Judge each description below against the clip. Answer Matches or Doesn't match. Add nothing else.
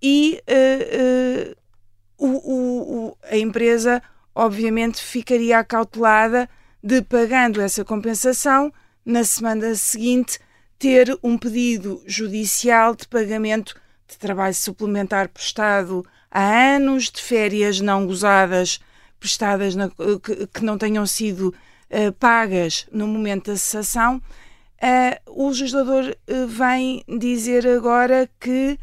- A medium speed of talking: Doesn't match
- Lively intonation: Doesn't match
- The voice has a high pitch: Matches